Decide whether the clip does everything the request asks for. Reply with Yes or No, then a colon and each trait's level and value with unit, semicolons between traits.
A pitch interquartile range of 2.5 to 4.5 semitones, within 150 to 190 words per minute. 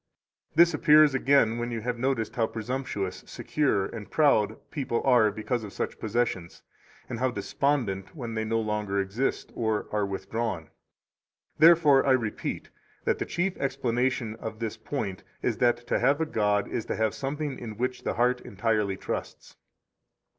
Yes: average, 3.9 semitones; average, 160 wpm